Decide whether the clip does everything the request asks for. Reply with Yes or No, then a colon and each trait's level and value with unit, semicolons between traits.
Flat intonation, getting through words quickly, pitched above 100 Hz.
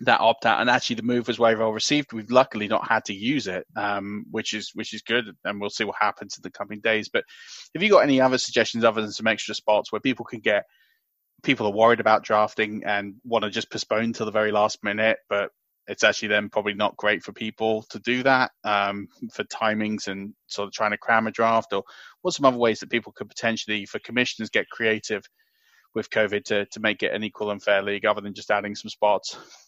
Yes: narrow, 1.7 semitones; fast, 235 wpm; low, 110 Hz